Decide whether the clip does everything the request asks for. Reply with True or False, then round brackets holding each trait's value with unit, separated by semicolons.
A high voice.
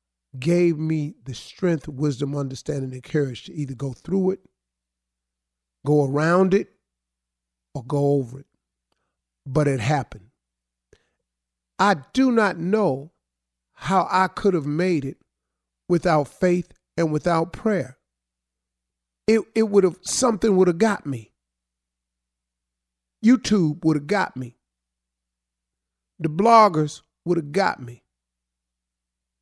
False (135 Hz)